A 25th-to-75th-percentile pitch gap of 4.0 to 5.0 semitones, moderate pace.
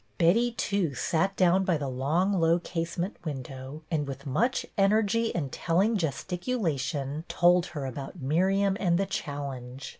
No: wide, 5.6 semitones; average, 150 wpm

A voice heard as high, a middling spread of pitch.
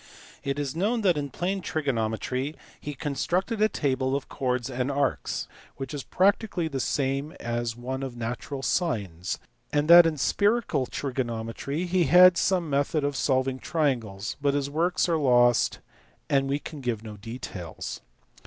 No: medium, 140 Hz; average, 4.6 semitones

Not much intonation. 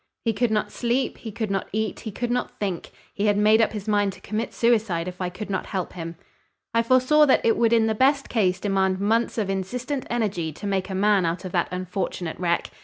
No: average, 3.6 semitones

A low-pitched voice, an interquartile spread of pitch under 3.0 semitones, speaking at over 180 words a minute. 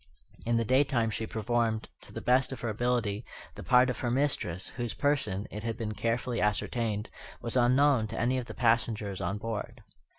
Yes: low, 115 Hz; narrow, 2.5 semitones; average, 190 wpm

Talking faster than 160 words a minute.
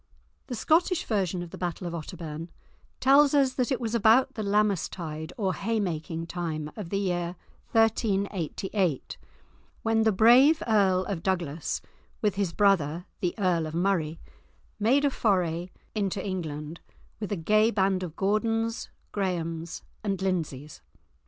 No: average, 145 wpm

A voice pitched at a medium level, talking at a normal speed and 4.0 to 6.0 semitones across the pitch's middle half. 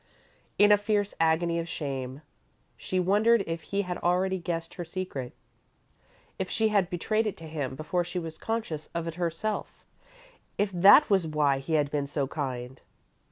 Yes: medium, 170 Hz; average, 170 wpm; average, 4.3 semitones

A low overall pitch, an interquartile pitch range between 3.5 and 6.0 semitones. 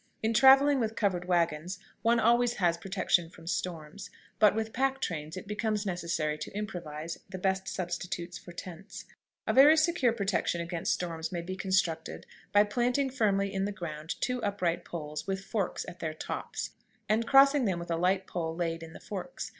No: high, 190 Hz; average, 4.4 semitones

